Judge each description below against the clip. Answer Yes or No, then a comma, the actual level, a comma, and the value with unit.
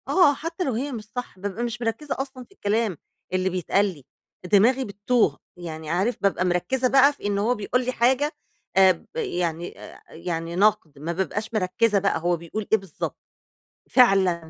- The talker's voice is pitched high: Yes, high, 205 Hz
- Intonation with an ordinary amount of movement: No, wide, 5.7 semitones